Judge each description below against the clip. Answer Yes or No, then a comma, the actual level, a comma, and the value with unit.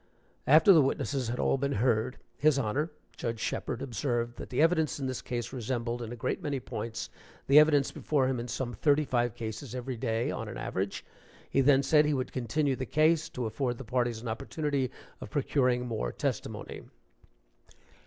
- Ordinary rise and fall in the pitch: Yes, average, 3.3 semitones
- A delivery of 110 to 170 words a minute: No, average, 185 wpm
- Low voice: Yes, low, 130 Hz